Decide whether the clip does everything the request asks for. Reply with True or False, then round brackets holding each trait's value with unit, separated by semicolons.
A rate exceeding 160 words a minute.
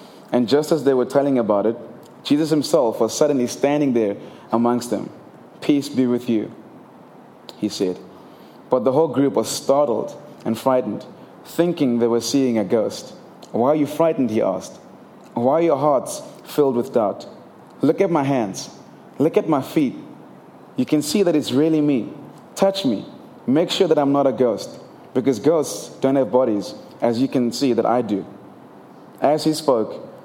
True (175 wpm)